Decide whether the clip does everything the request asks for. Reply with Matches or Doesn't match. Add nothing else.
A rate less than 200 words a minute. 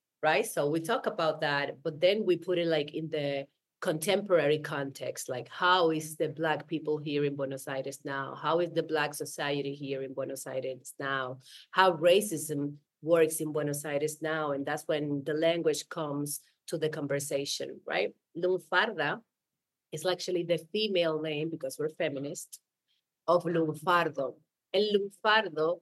Matches